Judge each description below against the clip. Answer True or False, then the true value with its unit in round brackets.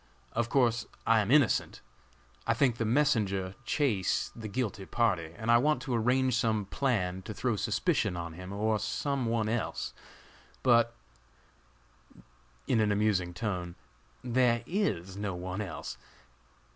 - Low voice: True (110 Hz)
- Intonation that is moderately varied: True (4.1 semitones)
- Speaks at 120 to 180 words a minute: True (140 wpm)